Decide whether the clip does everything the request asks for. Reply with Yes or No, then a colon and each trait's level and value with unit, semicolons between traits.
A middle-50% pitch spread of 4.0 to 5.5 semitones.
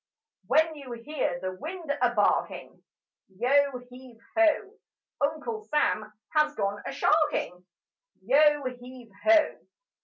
Yes: average, 4.8 semitones